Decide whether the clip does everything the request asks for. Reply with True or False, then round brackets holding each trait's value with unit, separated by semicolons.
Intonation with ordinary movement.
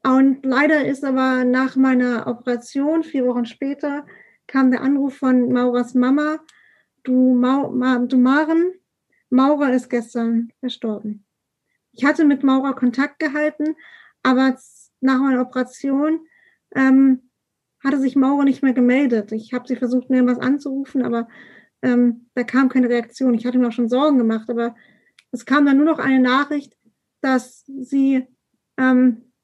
False (1.9 semitones)